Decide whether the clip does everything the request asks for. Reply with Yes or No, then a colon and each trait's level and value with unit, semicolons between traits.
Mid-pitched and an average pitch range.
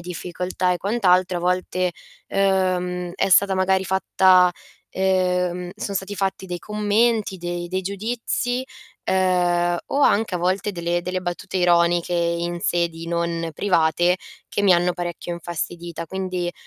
No: medium, 180 Hz; narrow, 1.6 semitones